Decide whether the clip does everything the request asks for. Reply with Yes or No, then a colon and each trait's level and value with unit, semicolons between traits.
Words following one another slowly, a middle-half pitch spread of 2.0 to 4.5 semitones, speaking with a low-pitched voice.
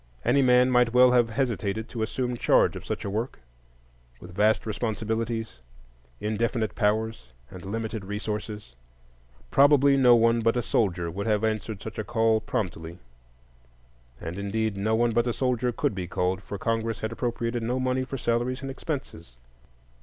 No: average, 160 wpm; average, 2.8 semitones; low, 115 Hz